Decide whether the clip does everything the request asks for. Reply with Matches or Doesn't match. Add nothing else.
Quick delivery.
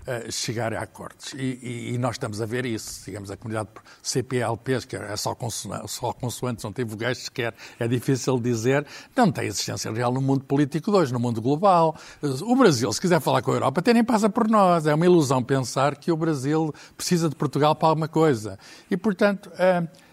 Matches